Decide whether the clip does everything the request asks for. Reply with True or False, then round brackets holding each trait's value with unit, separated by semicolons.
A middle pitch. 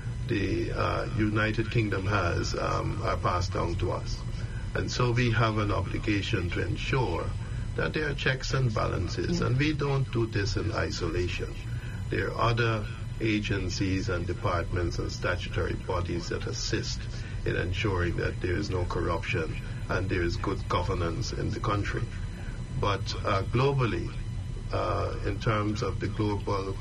False (110 Hz)